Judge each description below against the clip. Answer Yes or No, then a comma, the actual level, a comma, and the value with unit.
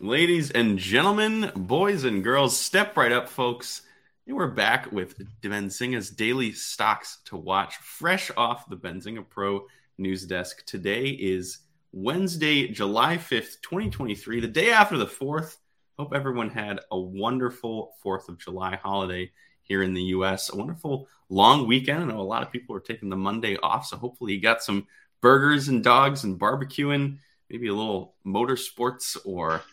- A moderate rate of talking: Yes, average, 160 wpm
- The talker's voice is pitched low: Yes, low, 115 Hz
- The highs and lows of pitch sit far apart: Yes, wide, 6.0 semitones